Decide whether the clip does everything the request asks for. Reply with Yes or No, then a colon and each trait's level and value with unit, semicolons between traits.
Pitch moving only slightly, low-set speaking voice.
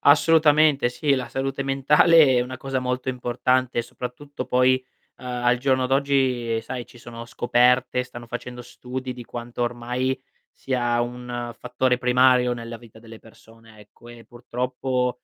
Yes: narrow, 1.4 semitones; low, 125 Hz